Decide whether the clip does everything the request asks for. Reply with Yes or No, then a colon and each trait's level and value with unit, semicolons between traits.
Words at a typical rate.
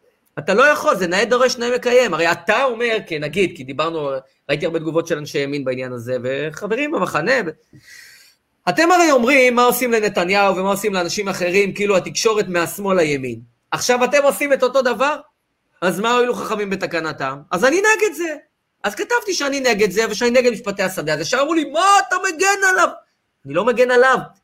No: fast, 185 wpm